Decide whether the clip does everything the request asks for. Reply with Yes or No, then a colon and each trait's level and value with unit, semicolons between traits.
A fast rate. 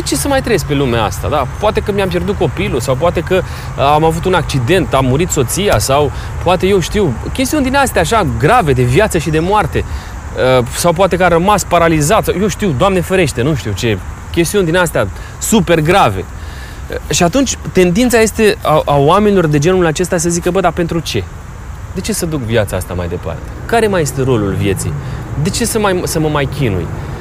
Yes: fast, 205 wpm